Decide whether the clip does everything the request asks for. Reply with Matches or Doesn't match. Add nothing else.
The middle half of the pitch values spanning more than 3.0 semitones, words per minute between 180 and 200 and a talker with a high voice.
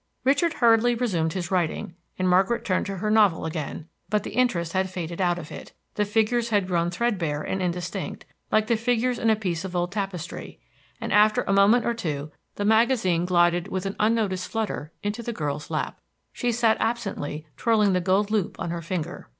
Matches